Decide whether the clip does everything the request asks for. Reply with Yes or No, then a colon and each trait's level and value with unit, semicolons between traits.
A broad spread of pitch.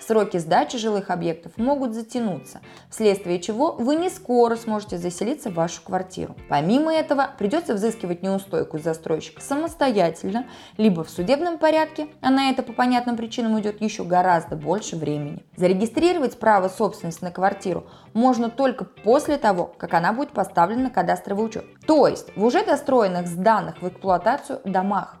Yes: wide, 6.2 semitones